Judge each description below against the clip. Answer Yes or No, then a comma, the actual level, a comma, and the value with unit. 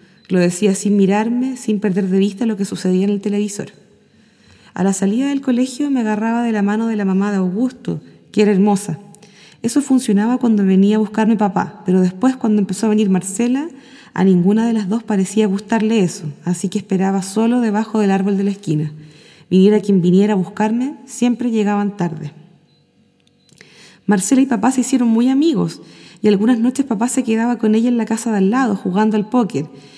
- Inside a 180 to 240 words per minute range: Yes, fast, 190 wpm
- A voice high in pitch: Yes, high, 210 Hz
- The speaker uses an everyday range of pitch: Yes, average, 3.3 semitones